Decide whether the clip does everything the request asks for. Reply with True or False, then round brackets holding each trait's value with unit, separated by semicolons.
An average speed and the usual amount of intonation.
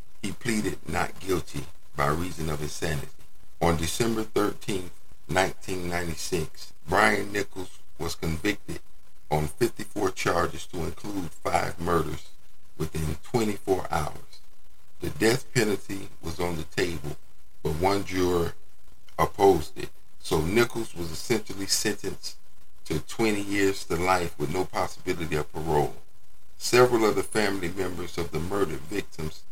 False (125 wpm; 4.0 semitones)